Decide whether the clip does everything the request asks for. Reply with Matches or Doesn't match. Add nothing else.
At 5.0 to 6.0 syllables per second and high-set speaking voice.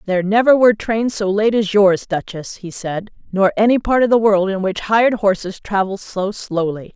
Matches